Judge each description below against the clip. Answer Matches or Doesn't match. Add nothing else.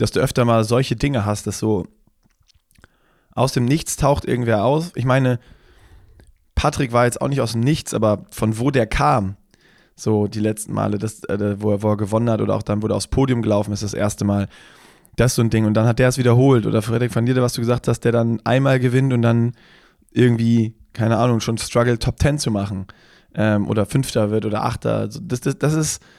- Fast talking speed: Matches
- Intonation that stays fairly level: Doesn't match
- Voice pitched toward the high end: Doesn't match